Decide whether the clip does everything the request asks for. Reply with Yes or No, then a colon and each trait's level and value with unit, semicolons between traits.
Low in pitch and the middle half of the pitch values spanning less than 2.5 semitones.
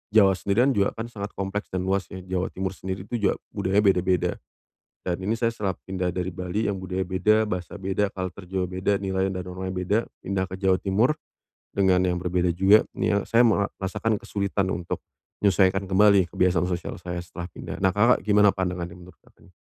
Yes: very low, 95 Hz; narrow, 1.8 semitones